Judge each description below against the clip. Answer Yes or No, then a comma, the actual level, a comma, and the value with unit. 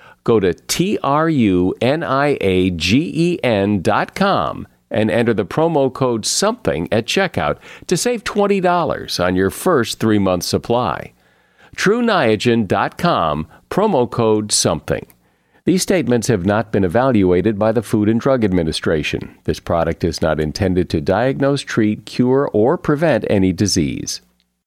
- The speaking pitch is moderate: No, low, 105 Hz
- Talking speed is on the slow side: Yes, slow, 120 wpm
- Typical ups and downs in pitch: No, wide, 5.7 semitones